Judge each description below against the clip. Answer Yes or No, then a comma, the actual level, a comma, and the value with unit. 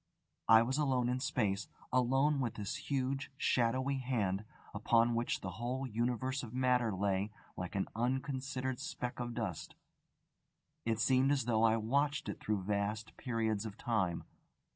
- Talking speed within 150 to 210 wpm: Yes, average, 155 wpm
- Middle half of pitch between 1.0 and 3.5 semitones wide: Yes, average, 3.2 semitones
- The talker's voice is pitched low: Yes, low, 120 Hz